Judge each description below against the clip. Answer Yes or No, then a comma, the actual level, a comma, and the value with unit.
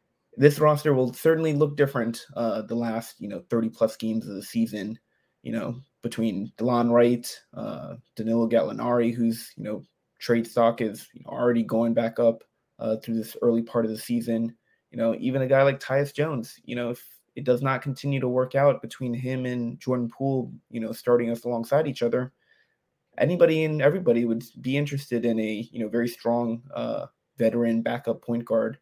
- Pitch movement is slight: Yes, narrow, 2.3 semitones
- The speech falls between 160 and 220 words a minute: Yes, average, 190 wpm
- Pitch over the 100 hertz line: Yes, low, 120 Hz